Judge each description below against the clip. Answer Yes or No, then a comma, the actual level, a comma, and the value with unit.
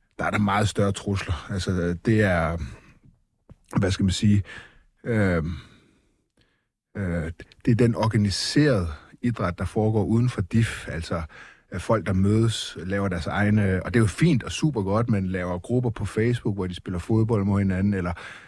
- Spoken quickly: No, average, 170 wpm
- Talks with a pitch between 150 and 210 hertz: No, low, 100 Hz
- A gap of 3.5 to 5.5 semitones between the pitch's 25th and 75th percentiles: No, average, 3.1 semitones